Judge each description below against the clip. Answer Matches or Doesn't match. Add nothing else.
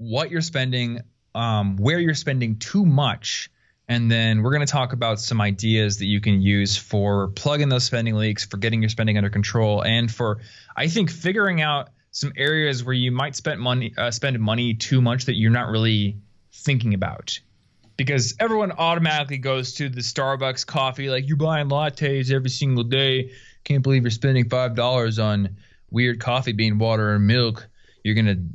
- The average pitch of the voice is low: Matches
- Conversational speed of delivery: Matches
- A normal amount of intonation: Matches